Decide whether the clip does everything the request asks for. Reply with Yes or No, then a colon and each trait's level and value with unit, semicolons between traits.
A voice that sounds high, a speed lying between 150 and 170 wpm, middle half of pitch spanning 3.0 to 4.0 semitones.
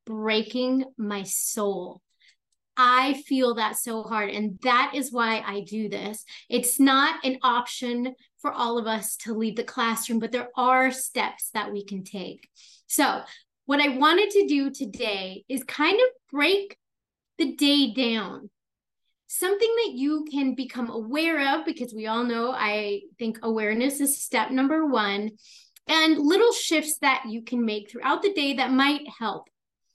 No: very high, 250 Hz; average, 160 wpm; average, 4.4 semitones